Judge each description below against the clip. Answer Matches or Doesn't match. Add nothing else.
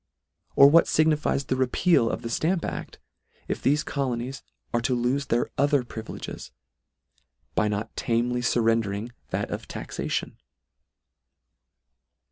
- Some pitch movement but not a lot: Matches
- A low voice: Matches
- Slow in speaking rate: Matches